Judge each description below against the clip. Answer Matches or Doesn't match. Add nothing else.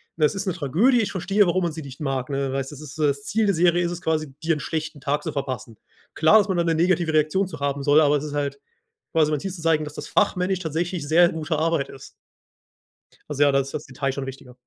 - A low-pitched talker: Doesn't match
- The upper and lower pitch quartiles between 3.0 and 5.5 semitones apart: Matches